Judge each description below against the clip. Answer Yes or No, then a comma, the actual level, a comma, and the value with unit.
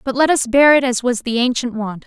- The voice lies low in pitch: No, very high, 250 Hz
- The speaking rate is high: Yes, fast, 290 wpm